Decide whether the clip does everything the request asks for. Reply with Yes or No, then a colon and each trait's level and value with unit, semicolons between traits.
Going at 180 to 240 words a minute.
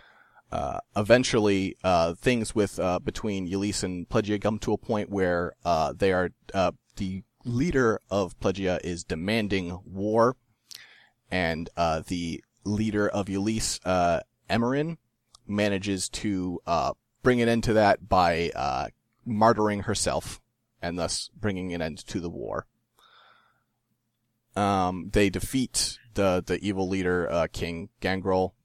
No: slow, 135 wpm